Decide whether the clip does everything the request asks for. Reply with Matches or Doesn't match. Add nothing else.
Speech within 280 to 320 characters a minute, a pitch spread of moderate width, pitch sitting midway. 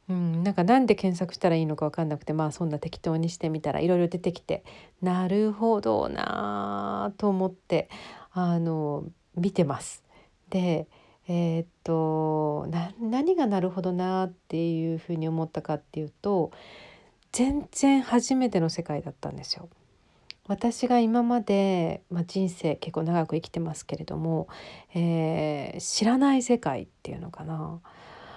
Matches